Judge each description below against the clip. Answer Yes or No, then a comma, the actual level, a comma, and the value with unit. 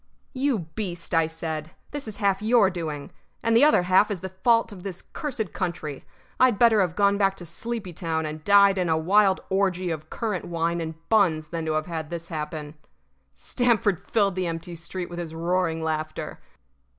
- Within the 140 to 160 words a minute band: No, average, 190 wpm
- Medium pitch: Yes, medium, 180 Hz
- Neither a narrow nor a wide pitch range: Yes, average, 3.9 semitones